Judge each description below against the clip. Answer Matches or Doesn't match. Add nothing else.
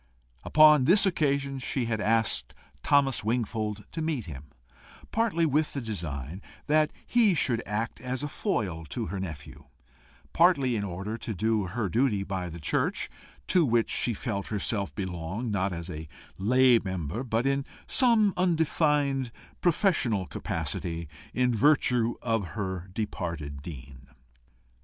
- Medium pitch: Doesn't match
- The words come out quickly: Doesn't match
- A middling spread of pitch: Doesn't match